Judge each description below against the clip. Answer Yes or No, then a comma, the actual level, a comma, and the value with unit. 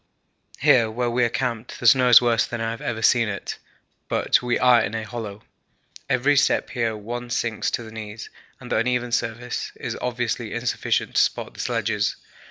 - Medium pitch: No, low, 120 Hz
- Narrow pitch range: Yes, narrow, 1.6 semitones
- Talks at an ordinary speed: Yes, average, 190 wpm